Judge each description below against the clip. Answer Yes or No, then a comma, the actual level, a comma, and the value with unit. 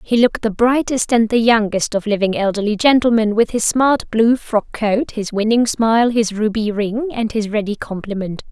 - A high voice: Yes, high, 220 Hz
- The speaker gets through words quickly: No, average, 190 wpm